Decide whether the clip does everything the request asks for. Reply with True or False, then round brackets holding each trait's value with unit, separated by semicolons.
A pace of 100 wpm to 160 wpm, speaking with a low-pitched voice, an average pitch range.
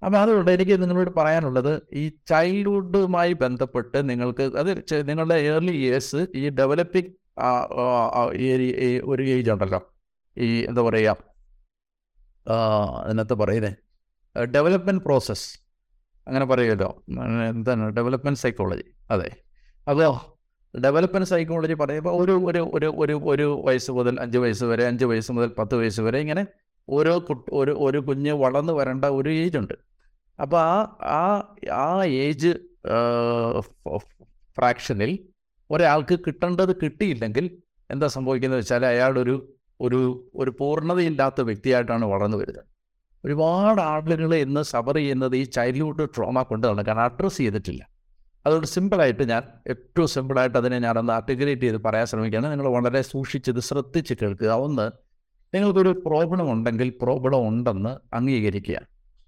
True (120 wpm; 130 Hz; 5.0 semitones)